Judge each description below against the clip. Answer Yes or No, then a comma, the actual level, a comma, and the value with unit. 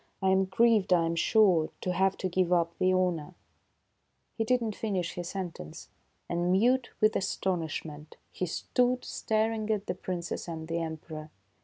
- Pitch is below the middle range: No, medium, 185 Hz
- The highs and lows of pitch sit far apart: No, average, 4.2 semitones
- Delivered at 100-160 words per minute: No, average, 180 wpm